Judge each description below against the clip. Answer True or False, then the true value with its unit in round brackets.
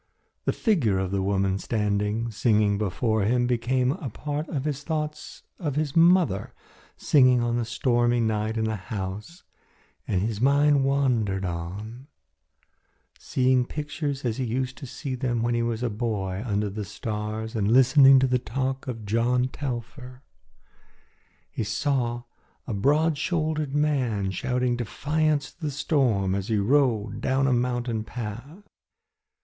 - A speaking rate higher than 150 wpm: False (145 wpm)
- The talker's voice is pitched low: True (120 Hz)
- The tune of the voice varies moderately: True (4.3 semitones)